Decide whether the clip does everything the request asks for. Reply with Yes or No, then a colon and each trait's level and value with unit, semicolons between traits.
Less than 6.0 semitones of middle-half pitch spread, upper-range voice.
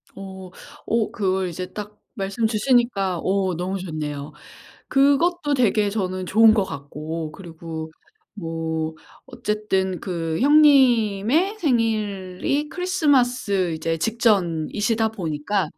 Yes: wide, 5.4 semitones; high, 195 Hz